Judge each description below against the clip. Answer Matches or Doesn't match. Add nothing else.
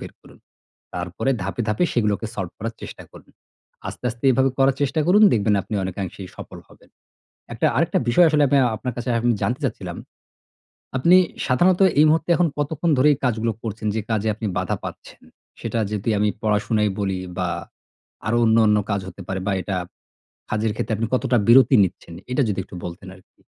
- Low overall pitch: Matches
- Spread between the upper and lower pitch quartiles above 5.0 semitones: Doesn't match